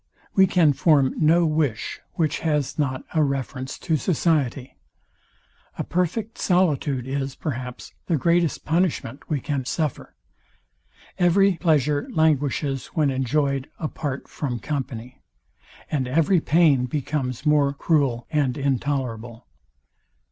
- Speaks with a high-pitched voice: No, medium, 145 Hz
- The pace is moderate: No, slow, 120 wpm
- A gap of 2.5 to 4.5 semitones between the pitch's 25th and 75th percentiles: Yes, average, 3.3 semitones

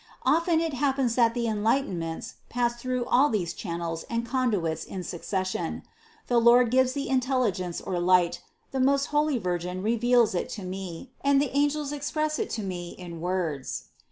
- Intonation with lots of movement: Yes, wide, 6.6 semitones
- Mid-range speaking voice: No, high, 235 Hz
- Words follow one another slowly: No, average, 165 wpm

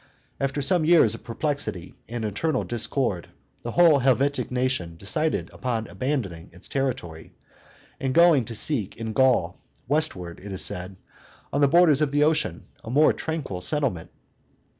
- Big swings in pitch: Yes, wide, 6.4 semitones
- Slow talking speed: No, average, 150 wpm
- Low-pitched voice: Yes, low, 130 Hz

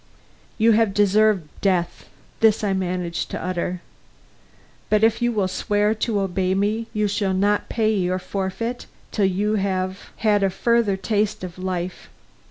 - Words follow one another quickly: No, average, 155 wpm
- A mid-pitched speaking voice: No, high, 200 Hz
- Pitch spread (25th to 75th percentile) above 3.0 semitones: No, narrow, 2.4 semitones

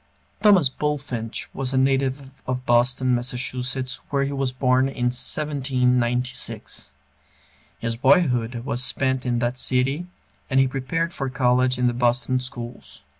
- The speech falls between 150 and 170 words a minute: No, slow, 135 wpm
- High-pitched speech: No, low, 130 Hz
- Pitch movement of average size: No, narrow, 1.5 semitones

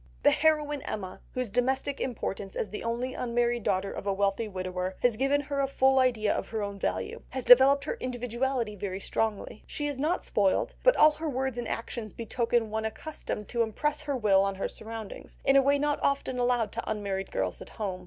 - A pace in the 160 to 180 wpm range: No, fast, 205 wpm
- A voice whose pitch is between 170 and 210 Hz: No, high, 235 Hz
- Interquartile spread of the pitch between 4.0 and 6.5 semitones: Yes, average, 4.7 semitones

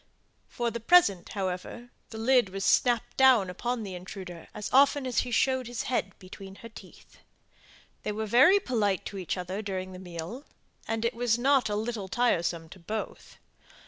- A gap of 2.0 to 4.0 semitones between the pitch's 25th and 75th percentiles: No, average, 4.5 semitones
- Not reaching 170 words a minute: No, average, 175 wpm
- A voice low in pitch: No, high, 220 Hz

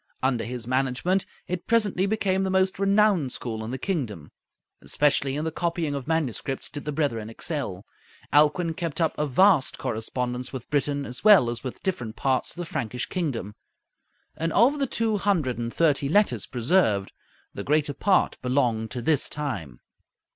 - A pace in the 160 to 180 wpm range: Yes, average, 170 wpm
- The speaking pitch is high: No, medium, 145 Hz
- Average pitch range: No, wide, 6.5 semitones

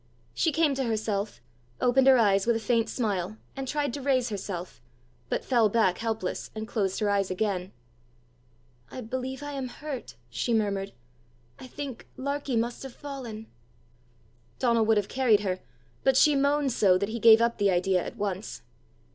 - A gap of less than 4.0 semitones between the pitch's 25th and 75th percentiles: No, average, 4.6 semitones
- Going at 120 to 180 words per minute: Yes, average, 170 wpm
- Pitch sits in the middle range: No, high, 225 Hz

